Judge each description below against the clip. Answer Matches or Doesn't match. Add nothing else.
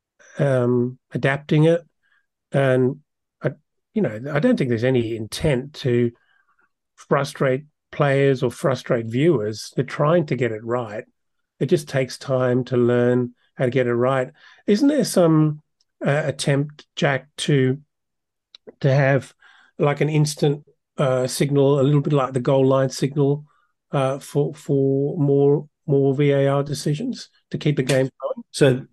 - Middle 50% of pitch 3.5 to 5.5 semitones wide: Doesn't match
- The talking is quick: Doesn't match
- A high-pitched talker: Doesn't match